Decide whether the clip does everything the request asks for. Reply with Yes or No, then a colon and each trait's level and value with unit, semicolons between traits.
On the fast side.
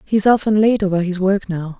Yes: fast, 235 wpm